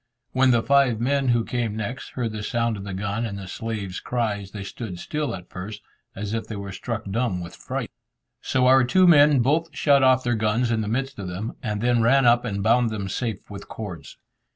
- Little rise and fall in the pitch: No, average, 3.8 semitones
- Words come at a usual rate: No, fast, 225 wpm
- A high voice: No, low, 115 Hz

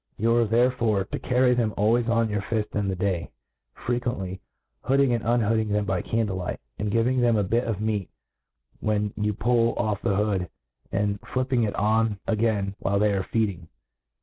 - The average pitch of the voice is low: Yes, low, 110 Hz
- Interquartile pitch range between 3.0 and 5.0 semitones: No, narrow, 2.6 semitones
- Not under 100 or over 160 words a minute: No, average, 185 wpm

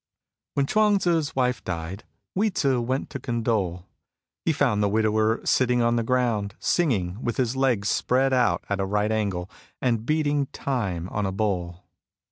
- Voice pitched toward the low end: Yes, low, 115 Hz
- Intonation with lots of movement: No, average, 4.7 semitones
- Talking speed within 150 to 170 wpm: Yes, average, 165 wpm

